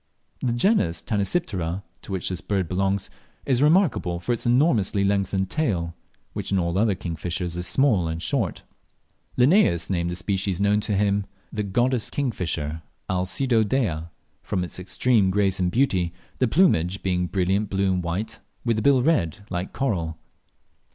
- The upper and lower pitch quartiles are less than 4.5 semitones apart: No, average, 4.8 semitones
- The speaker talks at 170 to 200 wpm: No, average, 160 wpm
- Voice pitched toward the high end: No, low, 100 Hz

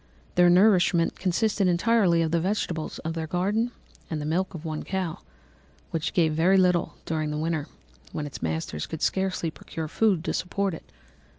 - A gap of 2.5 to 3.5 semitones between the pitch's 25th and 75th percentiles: Yes, average, 3.0 semitones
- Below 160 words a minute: No, average, 175 wpm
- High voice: No, medium, 170 Hz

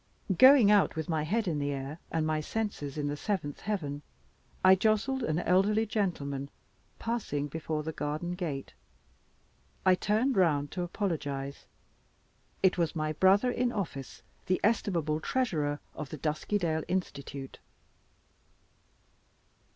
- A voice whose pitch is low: No, medium, 165 Hz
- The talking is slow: Yes, slow, 130 wpm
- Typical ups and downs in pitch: No, wide, 5.7 semitones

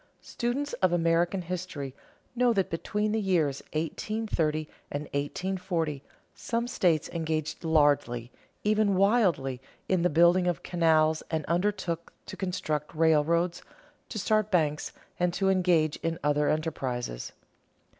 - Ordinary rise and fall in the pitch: Yes, average, 3.7 semitones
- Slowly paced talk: Yes, slow, 125 wpm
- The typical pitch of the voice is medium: Yes, medium, 170 Hz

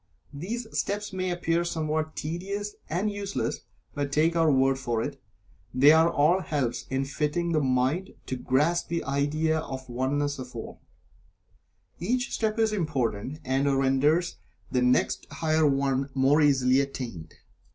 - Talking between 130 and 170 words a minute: Yes, average, 150 wpm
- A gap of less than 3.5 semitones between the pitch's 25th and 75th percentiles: No, average, 4.3 semitones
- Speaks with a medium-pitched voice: Yes, medium, 150 Hz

